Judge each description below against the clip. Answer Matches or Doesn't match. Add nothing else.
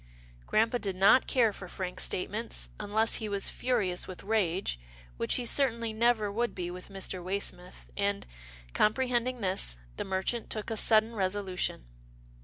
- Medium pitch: Doesn't match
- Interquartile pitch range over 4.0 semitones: Doesn't match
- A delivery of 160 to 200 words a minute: Doesn't match